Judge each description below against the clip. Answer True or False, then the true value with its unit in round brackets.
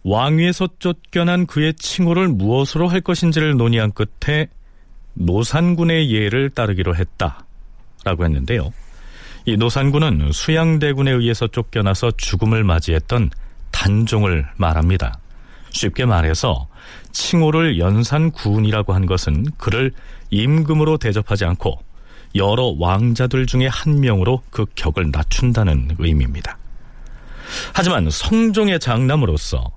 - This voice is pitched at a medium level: False (115 Hz)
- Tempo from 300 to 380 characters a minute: False (280 characters per minute)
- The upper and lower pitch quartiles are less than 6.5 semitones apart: False (8.3 semitones)